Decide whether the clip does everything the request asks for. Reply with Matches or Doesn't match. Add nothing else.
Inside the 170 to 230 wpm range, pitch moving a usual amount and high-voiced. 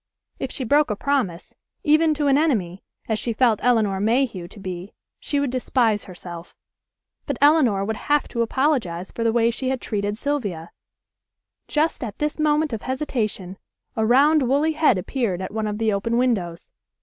Doesn't match